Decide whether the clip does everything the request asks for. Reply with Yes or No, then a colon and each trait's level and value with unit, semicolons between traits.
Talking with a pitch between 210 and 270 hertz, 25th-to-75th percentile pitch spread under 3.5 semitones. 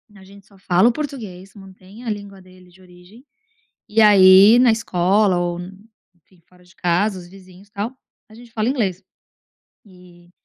No: high, 190 Hz; average, 2.9 semitones